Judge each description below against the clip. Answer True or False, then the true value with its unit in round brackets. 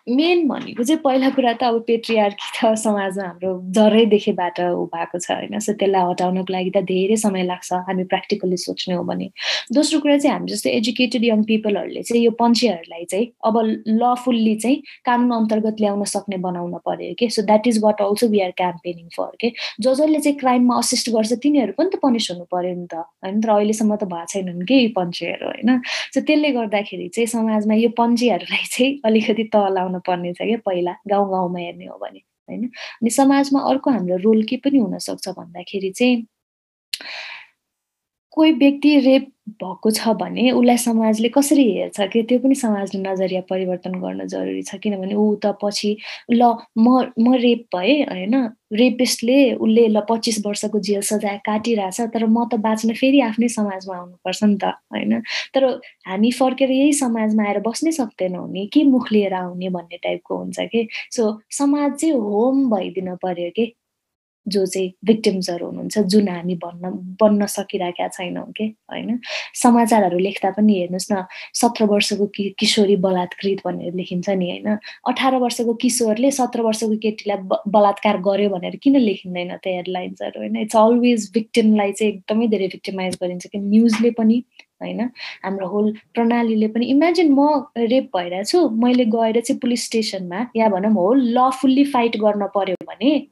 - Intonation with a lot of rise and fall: False (4.1 semitones)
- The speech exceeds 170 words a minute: False (165 wpm)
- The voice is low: False (220 Hz)